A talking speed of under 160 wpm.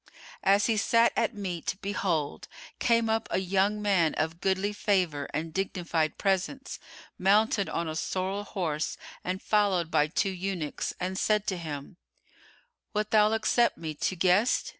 Yes: average, 150 wpm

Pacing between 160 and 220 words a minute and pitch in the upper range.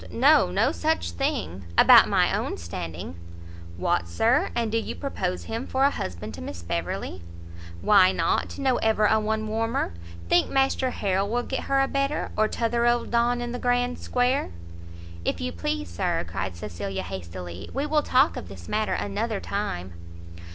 Yes: average, 170 wpm; high, 210 Hz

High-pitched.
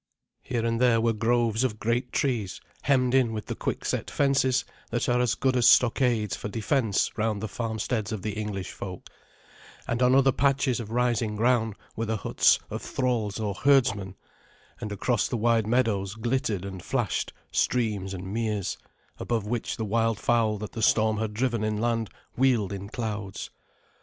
No: low, 115 Hz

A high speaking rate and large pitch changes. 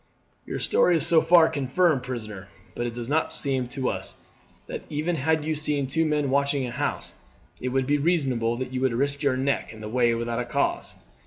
No: fast, 210 wpm; average, 3.5 semitones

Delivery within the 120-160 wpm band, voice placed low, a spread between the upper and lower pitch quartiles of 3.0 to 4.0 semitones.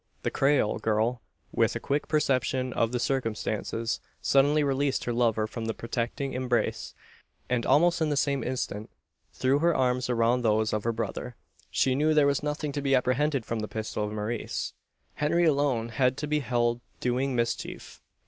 No: average, 175 wpm; low, 125 Hz; average, 3.4 semitones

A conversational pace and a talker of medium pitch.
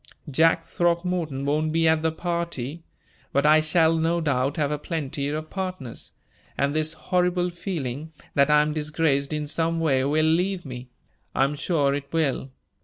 Yes: average, 170 wpm; medium, 155 Hz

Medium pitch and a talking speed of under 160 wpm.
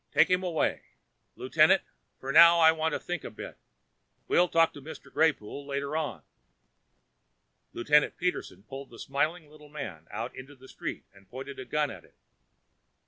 No: medium, 145 Hz; average, 165 wpm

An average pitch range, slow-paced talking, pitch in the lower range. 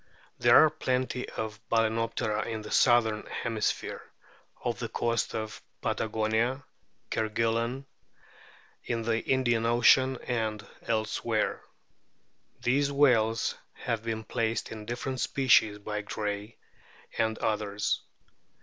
No: narrow, 1.8 semitones; slow, 105 wpm; low, 115 Hz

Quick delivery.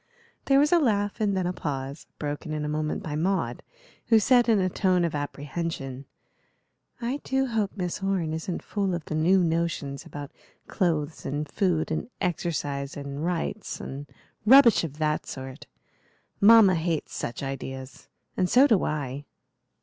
No: average, 160 wpm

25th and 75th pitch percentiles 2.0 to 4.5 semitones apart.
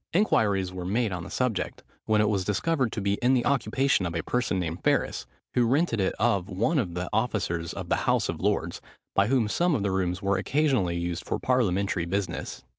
No: average, 5.2 semitones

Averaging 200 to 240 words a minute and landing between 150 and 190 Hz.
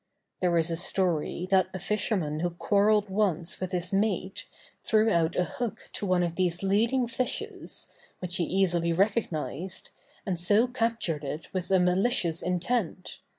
No: average, 155 wpm; medium, 185 Hz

